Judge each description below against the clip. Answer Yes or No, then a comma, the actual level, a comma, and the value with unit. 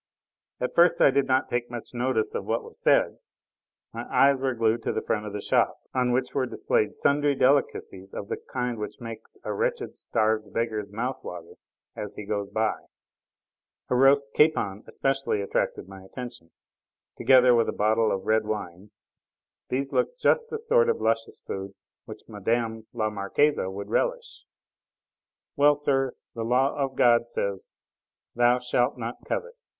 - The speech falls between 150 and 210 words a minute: Yes, average, 165 wpm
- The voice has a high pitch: No, low, 120 Hz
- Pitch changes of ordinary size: Yes, average, 4.2 semitones